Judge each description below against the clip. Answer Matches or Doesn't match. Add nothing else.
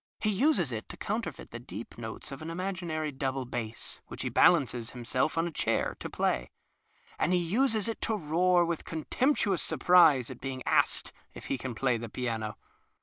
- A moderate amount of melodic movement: Doesn't match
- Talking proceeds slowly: Doesn't match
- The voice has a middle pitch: Matches